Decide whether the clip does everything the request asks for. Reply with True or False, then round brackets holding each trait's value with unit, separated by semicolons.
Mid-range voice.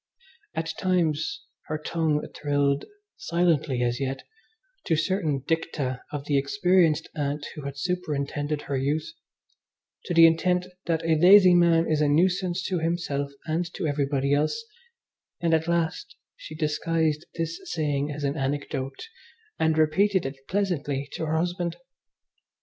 True (155 Hz)